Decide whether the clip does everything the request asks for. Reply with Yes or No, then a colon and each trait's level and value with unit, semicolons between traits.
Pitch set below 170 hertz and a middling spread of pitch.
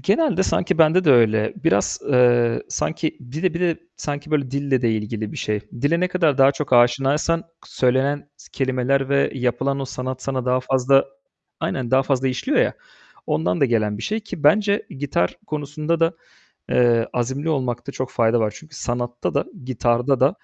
Yes: low, 135 Hz; average, 3.7 semitones